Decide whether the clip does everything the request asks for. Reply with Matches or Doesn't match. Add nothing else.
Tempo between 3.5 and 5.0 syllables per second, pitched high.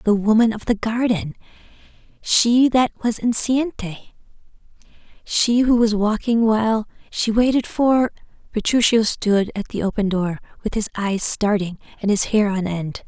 Matches